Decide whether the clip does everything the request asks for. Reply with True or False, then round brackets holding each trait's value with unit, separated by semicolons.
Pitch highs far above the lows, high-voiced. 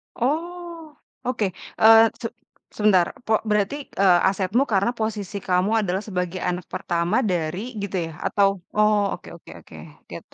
False (3.5 semitones; 205 Hz)